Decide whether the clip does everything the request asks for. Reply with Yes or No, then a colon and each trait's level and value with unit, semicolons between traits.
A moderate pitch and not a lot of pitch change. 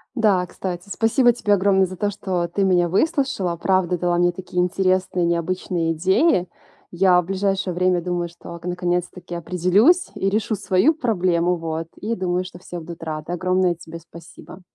Yes: medium, 180 Hz; narrow, 1.9 semitones